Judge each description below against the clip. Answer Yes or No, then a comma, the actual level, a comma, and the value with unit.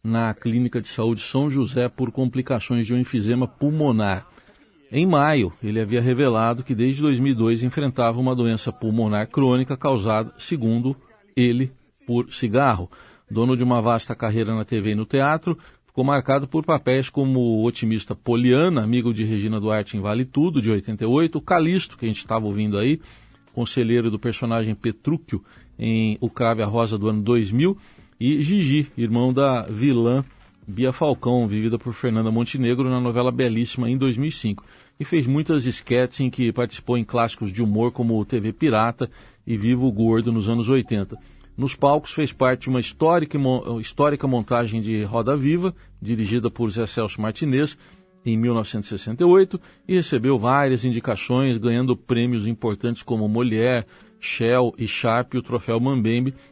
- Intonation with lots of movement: No, average, 3.0 semitones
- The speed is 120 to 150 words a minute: No, average, 160 wpm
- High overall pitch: No, low, 120 Hz